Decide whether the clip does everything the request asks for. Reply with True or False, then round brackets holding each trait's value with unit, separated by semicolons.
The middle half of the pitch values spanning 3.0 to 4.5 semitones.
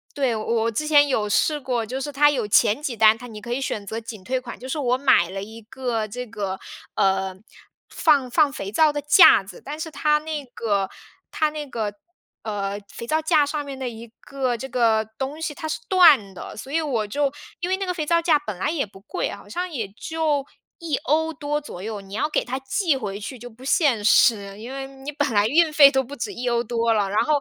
False (5.3 semitones)